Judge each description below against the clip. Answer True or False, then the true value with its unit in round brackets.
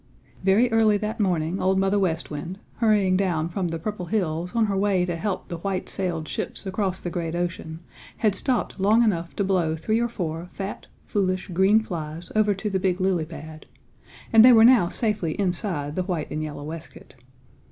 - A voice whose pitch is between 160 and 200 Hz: True (185 Hz)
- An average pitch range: True (3.7 semitones)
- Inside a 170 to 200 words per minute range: True (195 wpm)